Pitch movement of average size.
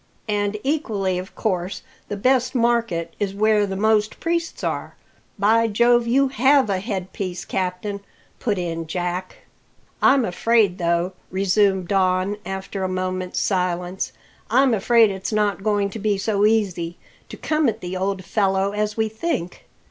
Yes: average, 3.2 semitones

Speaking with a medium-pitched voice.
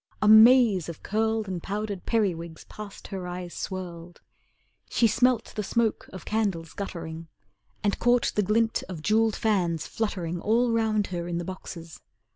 No: high, 200 Hz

